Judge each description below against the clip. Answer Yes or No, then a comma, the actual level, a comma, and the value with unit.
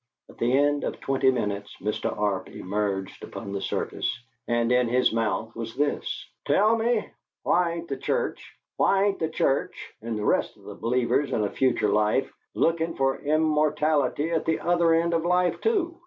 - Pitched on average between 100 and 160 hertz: Yes, low, 135 Hz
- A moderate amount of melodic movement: No, wide, 6.5 semitones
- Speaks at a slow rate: No, average, 180 wpm